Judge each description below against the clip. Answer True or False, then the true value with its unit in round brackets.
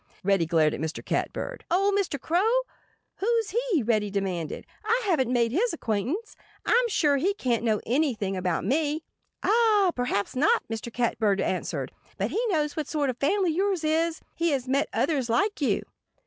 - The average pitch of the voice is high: True (290 Hz)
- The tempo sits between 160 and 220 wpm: True (170 wpm)